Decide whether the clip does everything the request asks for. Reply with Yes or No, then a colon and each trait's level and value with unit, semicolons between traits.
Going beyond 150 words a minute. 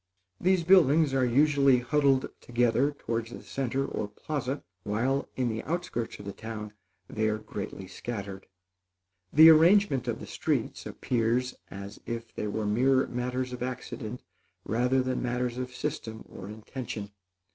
No: average, 145 wpm